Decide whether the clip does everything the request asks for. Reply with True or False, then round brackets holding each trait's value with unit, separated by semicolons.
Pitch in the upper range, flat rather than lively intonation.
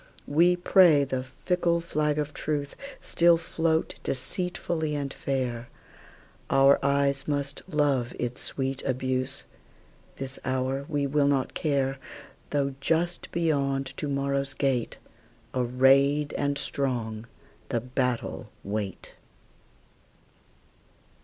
False (140 Hz; 2.3 semitones)